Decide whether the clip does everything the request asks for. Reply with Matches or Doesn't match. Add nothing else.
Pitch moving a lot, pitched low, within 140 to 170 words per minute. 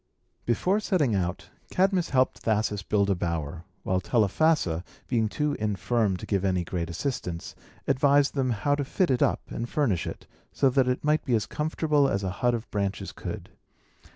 Doesn't match